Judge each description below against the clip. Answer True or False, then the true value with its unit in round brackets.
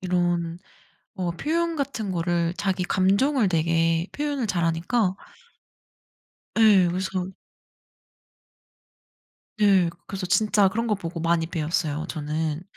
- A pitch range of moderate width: True (3.7 semitones)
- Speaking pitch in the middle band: True (180 Hz)